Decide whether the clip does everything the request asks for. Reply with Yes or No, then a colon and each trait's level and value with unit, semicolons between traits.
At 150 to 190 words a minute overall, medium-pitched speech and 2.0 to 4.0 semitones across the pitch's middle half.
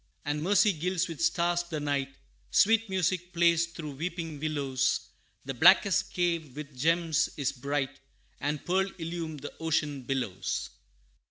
No: average, 140 wpm; medium, 160 Hz; average, 3.5 semitones